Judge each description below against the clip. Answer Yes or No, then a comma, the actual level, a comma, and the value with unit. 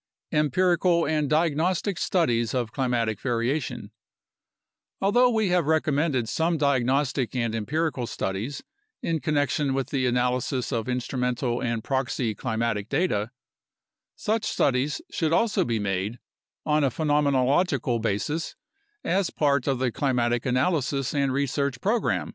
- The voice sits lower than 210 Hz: Yes, low, 135 Hz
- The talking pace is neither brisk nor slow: No, slow, 125 wpm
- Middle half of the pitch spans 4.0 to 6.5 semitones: Yes, average, 4.4 semitones